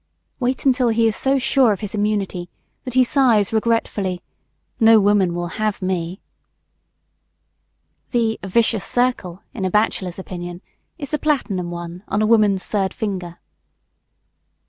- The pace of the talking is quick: No, average, 140 wpm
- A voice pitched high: Yes, high, 210 Hz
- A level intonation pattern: No, average, 4.0 semitones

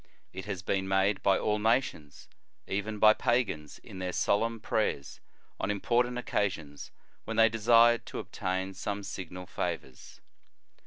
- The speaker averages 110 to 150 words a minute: Yes, average, 140 wpm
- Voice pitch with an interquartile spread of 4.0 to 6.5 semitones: No, average, 3.2 semitones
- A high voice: No, low, 100 Hz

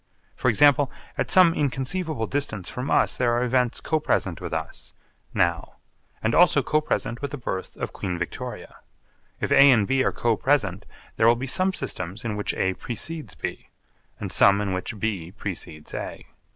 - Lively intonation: Yes, wide, 6.6 semitones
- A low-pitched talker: Yes, low, 120 Hz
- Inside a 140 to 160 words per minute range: No, average, 180 wpm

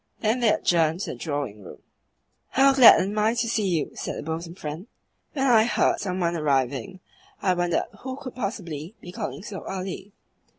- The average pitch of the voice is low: No, medium, 185 Hz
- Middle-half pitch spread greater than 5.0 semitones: Yes, wide, 5.4 semitones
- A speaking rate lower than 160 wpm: No, average, 185 wpm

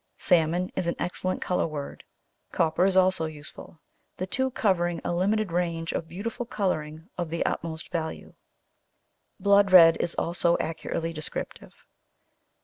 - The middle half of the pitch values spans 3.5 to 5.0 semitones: No, narrow, 2.4 semitones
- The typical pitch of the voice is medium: Yes, medium, 175 Hz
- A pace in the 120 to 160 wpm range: Yes, average, 140 wpm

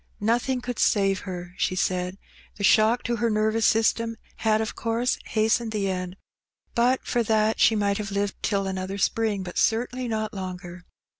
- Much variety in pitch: No, average, 2.9 semitones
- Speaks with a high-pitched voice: Yes, high, 215 Hz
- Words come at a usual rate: Yes, average, 170 wpm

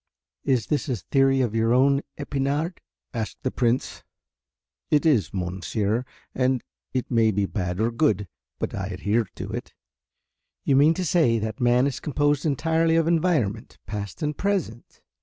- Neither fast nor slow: Yes, average, 160 wpm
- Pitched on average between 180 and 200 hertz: No, low, 125 Hz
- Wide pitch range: No, average, 5.0 semitones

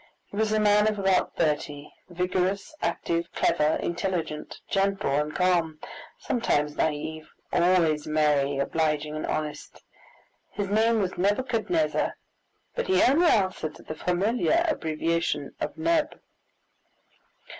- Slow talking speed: Yes, slow, 120 wpm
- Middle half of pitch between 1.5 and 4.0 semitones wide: No, wide, 5.4 semitones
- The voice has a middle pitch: Yes, medium, 180 Hz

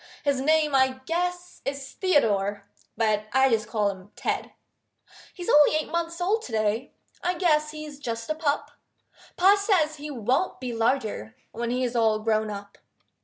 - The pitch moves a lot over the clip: Yes, wide, 6.1 semitones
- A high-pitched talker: Yes, very high, 265 Hz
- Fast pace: No, average, 170 wpm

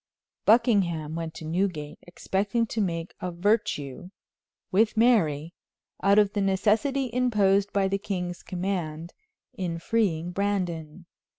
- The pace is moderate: No, slow, 120 wpm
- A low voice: No, high, 190 Hz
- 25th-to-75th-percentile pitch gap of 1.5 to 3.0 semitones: No, average, 3.8 semitones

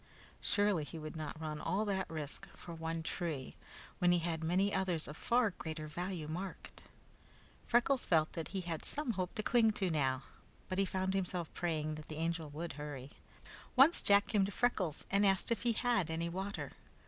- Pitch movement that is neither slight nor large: Yes, average, 3.9 semitones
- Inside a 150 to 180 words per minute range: No, average, 190 wpm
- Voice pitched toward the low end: No, medium, 175 Hz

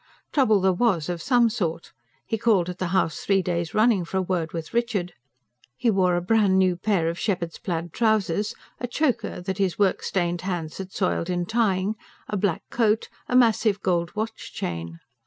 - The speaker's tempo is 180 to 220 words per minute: Yes, average, 190 wpm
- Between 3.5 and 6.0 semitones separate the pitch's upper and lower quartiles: Yes, average, 3.8 semitones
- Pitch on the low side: No, high, 190 Hz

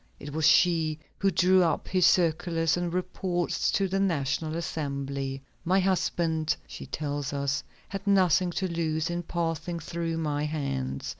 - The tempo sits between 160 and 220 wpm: No, average, 150 wpm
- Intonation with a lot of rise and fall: No, average, 3.1 semitones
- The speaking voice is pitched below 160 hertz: No, medium, 165 Hz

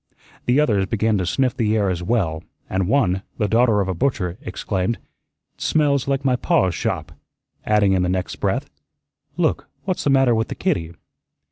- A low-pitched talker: Yes, low, 105 Hz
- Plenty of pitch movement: Yes, wide, 5.7 semitones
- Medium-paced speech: Yes, average, 175 wpm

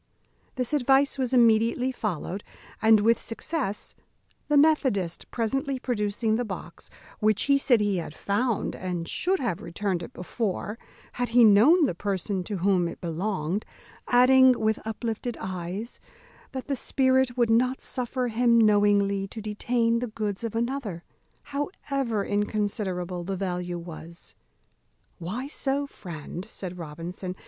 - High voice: Yes, high, 215 Hz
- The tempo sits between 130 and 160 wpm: Yes, average, 140 wpm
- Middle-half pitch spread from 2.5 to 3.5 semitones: No, average, 4.9 semitones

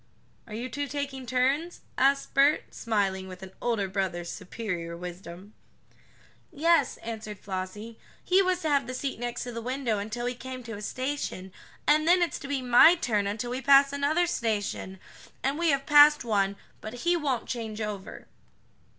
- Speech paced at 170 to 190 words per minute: Yes, average, 175 wpm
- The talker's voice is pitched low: No, high, 245 Hz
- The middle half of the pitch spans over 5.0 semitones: Yes, wide, 5.5 semitones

